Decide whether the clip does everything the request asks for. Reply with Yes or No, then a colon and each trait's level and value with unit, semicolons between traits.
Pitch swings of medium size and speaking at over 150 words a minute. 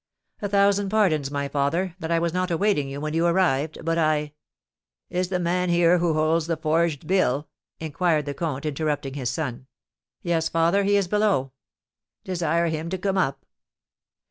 Yes: average, 3.4 semitones; average, 175 wpm